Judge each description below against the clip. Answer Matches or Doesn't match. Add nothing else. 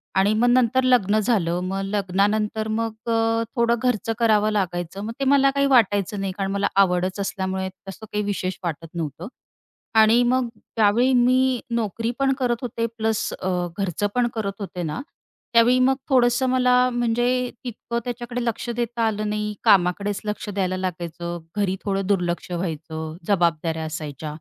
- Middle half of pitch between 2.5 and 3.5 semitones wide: Doesn't match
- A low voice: Doesn't match